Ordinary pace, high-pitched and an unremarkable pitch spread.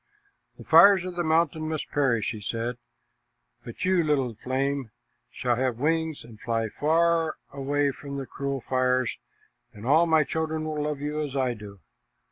No: average, 170 wpm; medium, 140 Hz; average, 4.1 semitones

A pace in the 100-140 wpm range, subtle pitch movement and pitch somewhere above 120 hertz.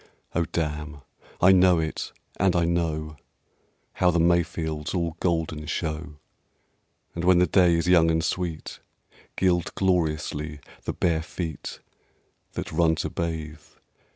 No: slow, 135 wpm; narrow, 2.0 semitones; very low, 85 Hz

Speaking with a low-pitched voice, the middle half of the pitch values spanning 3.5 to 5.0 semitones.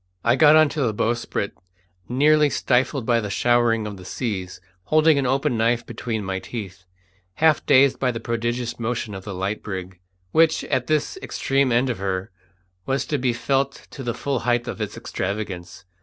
Yes: low, 120 Hz; average, 4.5 semitones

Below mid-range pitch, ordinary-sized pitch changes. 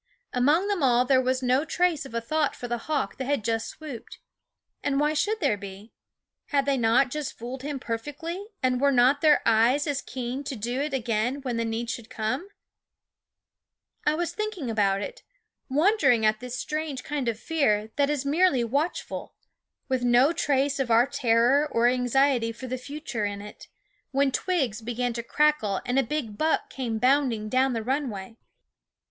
No: very high, 260 Hz; average, 3.9 semitones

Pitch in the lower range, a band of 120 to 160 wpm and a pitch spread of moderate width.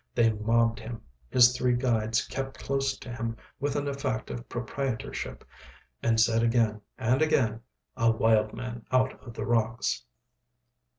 No: low, 120 Hz; average, 145 wpm; narrow, 2.2 semitones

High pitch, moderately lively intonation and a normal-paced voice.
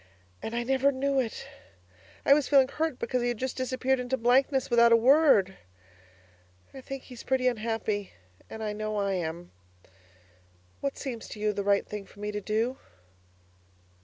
Yes: high, 240 Hz; average, 3.8 semitones; average, 170 wpm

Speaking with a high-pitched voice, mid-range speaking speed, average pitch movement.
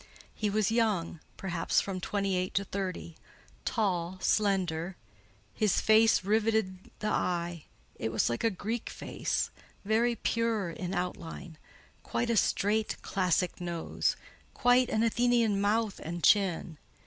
No: high, 195 Hz; slow, 125 wpm; average, 3.7 semitones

